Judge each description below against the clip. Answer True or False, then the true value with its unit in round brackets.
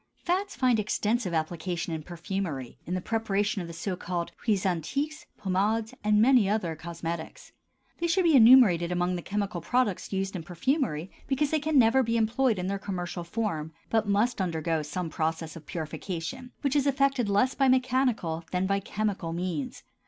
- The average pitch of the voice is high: True (195 Hz)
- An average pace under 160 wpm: False (175 wpm)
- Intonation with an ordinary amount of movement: False (6.3 semitones)